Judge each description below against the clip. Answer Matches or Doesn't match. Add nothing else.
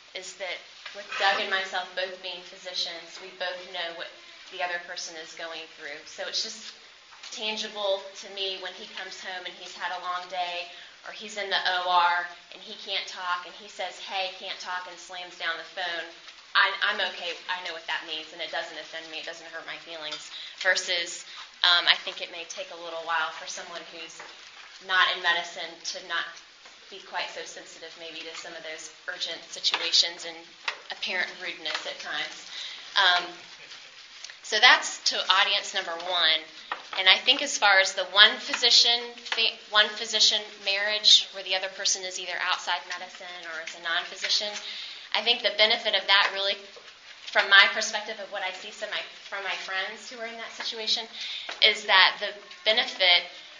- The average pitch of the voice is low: Doesn't match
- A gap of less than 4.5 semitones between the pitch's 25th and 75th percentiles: Matches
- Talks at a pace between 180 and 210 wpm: Matches